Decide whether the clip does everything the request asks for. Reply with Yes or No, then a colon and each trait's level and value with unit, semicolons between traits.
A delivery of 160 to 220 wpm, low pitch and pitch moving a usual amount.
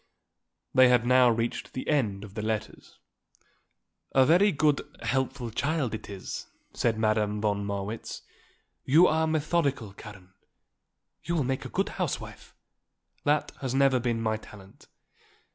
No: average, 140 wpm; low, 120 Hz; average, 4.7 semitones